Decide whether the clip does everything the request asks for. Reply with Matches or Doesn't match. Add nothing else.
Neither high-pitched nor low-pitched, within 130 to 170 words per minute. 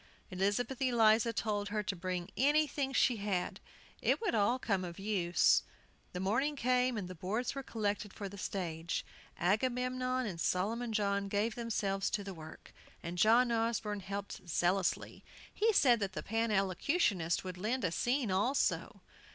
Doesn't match